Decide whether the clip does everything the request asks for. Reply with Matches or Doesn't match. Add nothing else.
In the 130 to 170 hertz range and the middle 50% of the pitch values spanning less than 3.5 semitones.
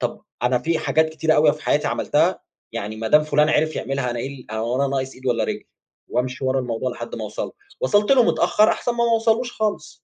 Doesn't match